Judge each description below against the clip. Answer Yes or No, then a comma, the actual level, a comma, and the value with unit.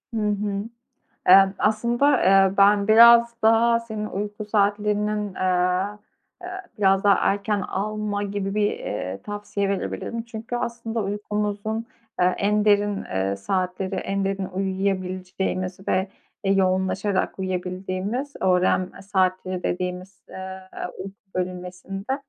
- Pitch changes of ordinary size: No, narrow, 2.1 semitones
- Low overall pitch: No, high, 200 Hz